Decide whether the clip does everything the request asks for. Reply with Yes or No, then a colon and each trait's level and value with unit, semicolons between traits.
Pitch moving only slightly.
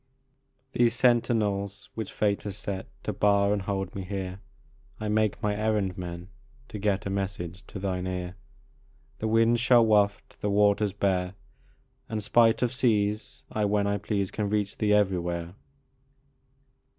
Yes: narrow, 1.9 semitones